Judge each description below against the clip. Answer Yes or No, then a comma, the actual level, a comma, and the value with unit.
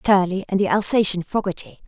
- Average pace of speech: Yes, average, 160 wpm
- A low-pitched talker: No, medium, 185 Hz